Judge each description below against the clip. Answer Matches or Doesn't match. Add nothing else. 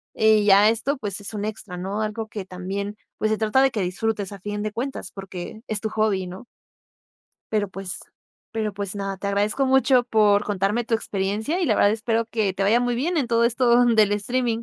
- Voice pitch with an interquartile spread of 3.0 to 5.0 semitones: Doesn't match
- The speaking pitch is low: Doesn't match